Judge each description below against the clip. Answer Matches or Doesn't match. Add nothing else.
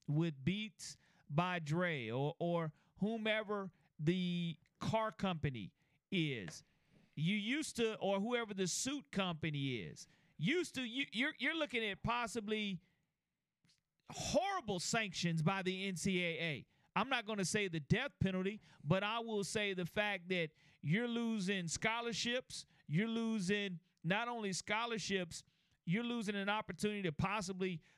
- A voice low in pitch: Doesn't match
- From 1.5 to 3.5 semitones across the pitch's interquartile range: Doesn't match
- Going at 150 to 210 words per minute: Doesn't match